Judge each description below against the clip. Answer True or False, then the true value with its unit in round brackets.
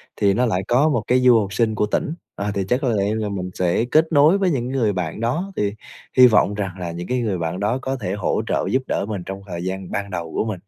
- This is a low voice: True (105 Hz)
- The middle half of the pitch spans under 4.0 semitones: False (4.7 semitones)